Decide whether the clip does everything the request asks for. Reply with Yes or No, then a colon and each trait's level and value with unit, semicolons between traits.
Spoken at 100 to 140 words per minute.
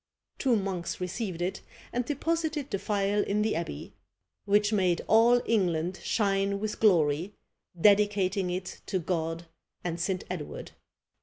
Yes: slow, 135 wpm